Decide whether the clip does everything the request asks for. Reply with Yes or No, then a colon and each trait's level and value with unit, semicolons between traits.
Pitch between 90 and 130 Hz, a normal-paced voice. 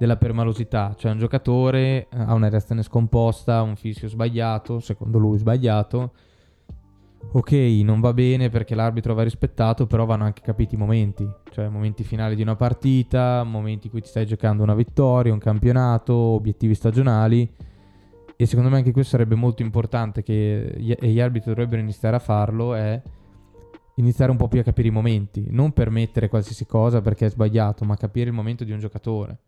No: low, 115 Hz; fast, 175 wpm